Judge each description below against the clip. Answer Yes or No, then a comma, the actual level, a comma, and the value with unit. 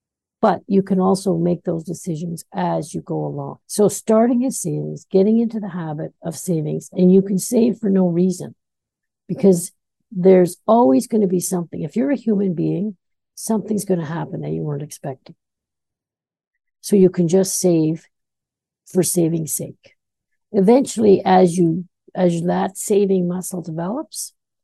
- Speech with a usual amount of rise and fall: Yes, average, 3.1 semitones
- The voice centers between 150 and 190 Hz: Yes, medium, 185 Hz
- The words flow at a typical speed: Yes, average, 155 wpm